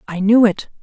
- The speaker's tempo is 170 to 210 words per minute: No, fast, 220 wpm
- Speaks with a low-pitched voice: No, high, 210 Hz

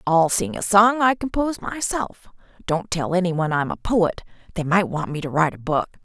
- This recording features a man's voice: No, female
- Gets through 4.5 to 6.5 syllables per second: Yes, 5.3 syllables/s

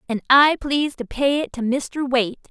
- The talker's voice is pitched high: Yes, very high, 265 Hz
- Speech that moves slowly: No, fast, 215 wpm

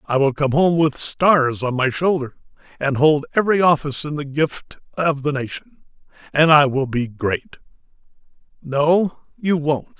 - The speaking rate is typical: Yes, average, 160 wpm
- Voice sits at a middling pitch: Yes, medium, 150 Hz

